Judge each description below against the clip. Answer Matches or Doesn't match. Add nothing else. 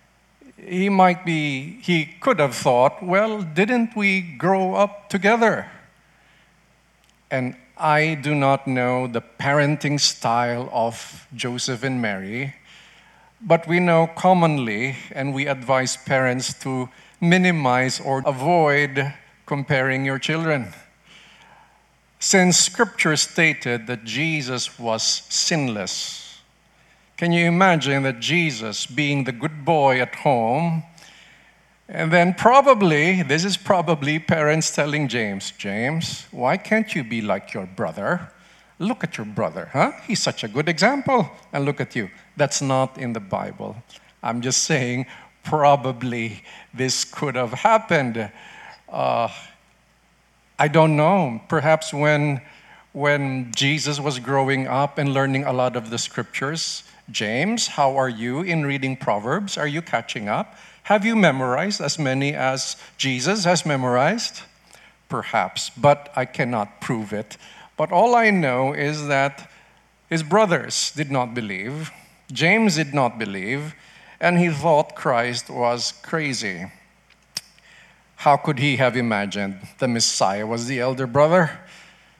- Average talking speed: Doesn't match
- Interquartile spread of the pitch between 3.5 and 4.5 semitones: Doesn't match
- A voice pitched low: Doesn't match